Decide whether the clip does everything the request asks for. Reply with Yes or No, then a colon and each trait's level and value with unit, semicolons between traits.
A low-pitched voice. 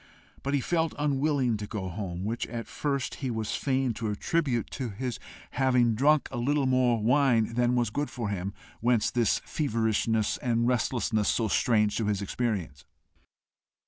Yes: low, 120 Hz